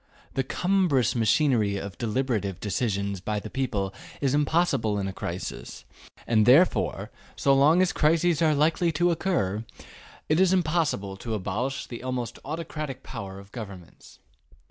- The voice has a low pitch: Yes, low, 125 Hz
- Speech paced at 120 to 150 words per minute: Yes, average, 145 wpm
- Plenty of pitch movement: Yes, wide, 7.3 semitones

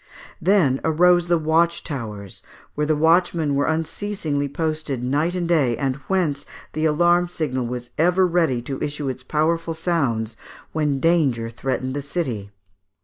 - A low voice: No, medium, 155 Hz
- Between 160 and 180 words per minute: No, average, 145 wpm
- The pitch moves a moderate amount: Yes, average, 4.4 semitones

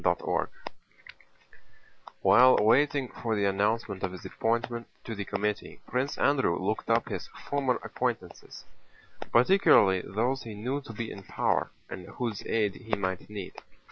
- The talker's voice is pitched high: No, low, 115 Hz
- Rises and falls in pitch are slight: No, average, 4.0 semitones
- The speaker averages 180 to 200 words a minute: No, average, 145 wpm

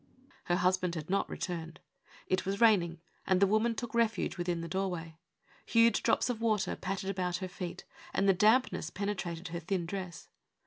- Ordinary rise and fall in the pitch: Yes, average, 3.0 semitones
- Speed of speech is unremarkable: Yes, average, 180 wpm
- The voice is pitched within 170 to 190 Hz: Yes, medium, 185 Hz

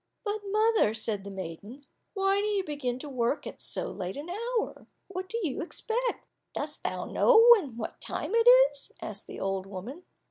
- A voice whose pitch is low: No, very high, 295 Hz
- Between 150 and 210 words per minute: Yes, average, 180 wpm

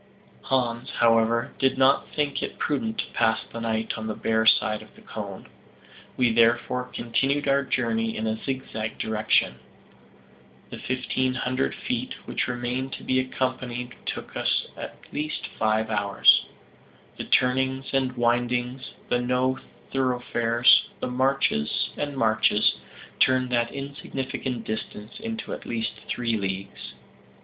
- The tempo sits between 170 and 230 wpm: No, slow, 135 wpm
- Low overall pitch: Yes, low, 125 Hz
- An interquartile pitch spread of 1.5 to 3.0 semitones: Yes, average, 2.7 semitones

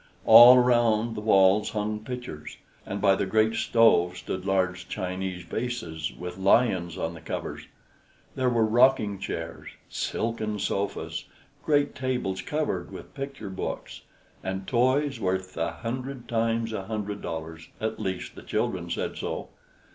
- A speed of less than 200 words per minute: Yes, average, 140 wpm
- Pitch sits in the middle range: No, low, 105 Hz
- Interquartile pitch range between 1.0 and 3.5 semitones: No, average, 4.2 semitones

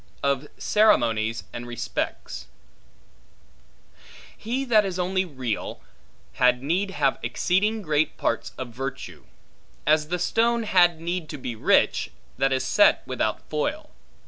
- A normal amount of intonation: No, wide, 6.6 semitones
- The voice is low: No, medium, 155 Hz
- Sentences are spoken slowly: Yes, slow, 125 wpm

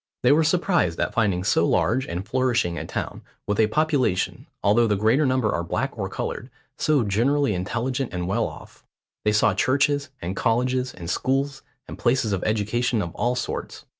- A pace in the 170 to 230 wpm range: Yes, average, 180 wpm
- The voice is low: Yes, low, 120 Hz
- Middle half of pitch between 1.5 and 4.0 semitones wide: No, average, 4.6 semitones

